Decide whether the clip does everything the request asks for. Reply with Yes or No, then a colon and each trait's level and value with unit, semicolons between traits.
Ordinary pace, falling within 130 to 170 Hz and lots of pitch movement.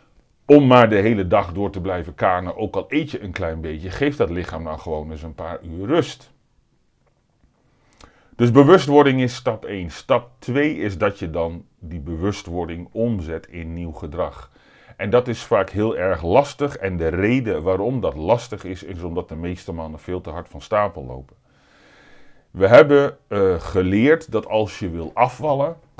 No: average, 180 wpm; very low, 95 Hz; wide, 6.4 semitones